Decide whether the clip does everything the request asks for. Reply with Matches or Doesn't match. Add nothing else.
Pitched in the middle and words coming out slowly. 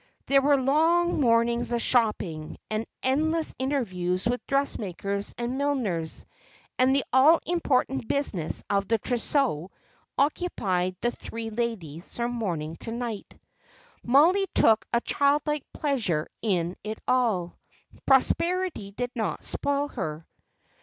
Doesn't match